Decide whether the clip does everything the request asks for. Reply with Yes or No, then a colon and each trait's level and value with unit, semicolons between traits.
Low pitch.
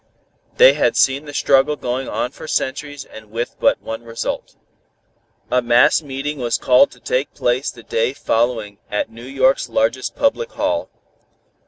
Yes: low, 130 Hz